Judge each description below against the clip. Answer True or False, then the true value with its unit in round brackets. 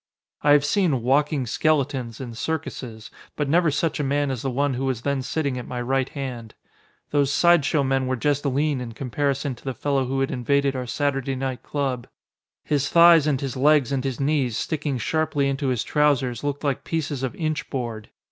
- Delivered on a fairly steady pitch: True (2.3 semitones)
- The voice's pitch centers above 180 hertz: False (135 Hz)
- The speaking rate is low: False (200 wpm)